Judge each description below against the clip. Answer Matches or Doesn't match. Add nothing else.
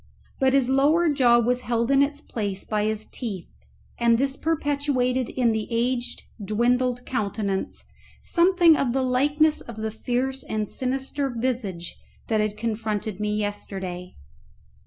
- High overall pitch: Matches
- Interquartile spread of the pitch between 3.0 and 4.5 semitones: Matches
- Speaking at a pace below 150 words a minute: Matches